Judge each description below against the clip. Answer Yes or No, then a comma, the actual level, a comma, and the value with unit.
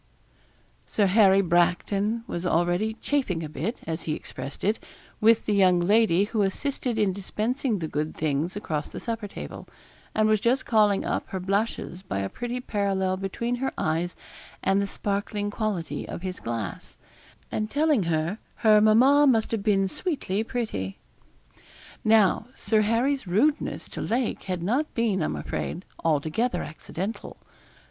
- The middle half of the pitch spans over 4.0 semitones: Yes, average, 4.4 semitones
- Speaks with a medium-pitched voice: No, high, 200 Hz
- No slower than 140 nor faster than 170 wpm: Yes, average, 155 wpm